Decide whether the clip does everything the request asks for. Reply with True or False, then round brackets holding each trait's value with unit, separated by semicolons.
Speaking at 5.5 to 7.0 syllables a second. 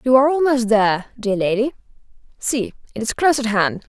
True (6.0 syllables/s)